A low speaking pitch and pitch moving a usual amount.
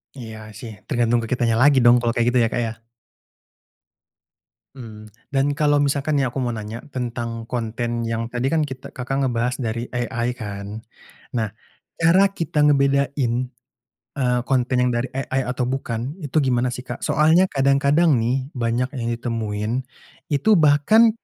Yes: low, 125 Hz; average, 3.0 semitones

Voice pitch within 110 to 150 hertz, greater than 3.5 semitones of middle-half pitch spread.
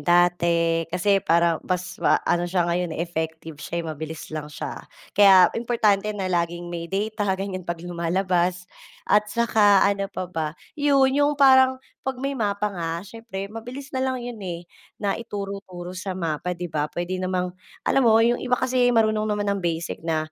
No: medium, 185 Hz; average, 4.0 semitones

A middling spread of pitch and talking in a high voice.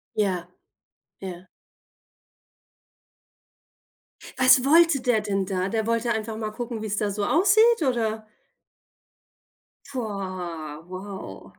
Yes: average, 4.3 semitones; high, 215 Hz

